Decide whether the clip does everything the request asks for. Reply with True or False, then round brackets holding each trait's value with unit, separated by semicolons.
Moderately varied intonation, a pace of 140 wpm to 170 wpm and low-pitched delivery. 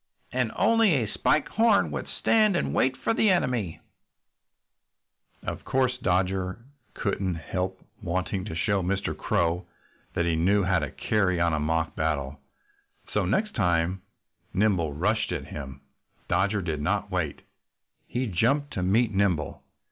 True (4.6 semitones; 150 wpm; 95 Hz)